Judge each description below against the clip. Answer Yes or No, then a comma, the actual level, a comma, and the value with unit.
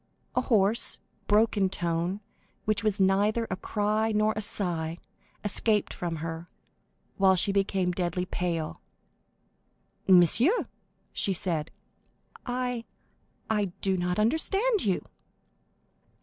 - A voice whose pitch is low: No, high, 195 Hz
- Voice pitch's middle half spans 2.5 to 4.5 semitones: Yes, average, 3.5 semitones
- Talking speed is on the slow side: Yes, slow, 105 wpm